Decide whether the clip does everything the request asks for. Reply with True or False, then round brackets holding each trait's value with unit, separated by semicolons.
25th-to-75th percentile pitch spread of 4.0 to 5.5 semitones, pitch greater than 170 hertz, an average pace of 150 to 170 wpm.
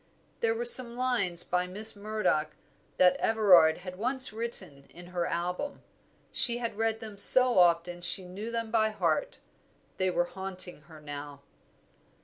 True (4.7 semitones; 190 Hz; 155 wpm)